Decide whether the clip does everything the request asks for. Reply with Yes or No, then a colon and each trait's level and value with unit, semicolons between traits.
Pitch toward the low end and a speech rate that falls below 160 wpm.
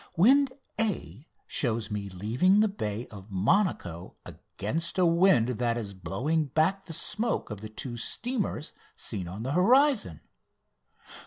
Yes: low, 130 Hz; average, 140 wpm